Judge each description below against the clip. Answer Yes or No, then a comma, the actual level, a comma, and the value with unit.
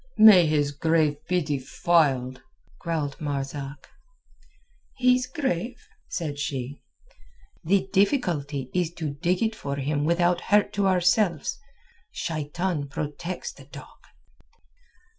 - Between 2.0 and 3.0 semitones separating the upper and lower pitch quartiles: No, average, 4.3 semitones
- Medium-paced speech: No, slow, 105 wpm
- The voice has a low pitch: No, medium, 160 Hz